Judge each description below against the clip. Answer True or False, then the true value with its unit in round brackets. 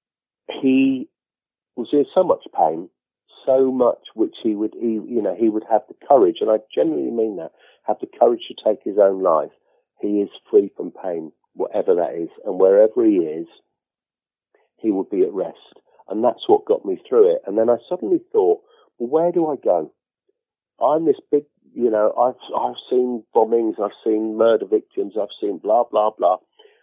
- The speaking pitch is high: True (335 Hz)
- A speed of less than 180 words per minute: False (190 wpm)